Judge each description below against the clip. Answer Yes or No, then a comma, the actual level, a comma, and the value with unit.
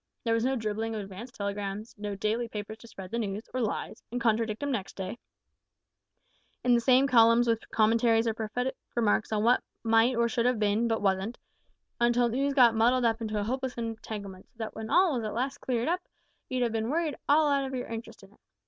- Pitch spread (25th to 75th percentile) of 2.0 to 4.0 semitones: Yes, narrow, 2.4 semitones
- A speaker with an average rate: No, fast, 215 wpm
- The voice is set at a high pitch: Yes, high, 230 Hz